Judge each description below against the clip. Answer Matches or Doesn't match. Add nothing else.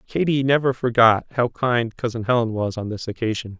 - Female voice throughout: Doesn't match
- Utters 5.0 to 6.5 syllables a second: Matches